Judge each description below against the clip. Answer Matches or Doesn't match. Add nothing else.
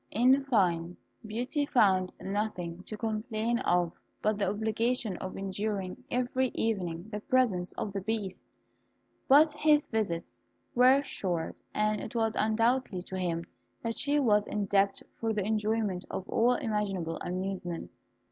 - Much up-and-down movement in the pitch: Doesn't match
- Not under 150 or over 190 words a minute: Doesn't match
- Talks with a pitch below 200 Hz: Doesn't match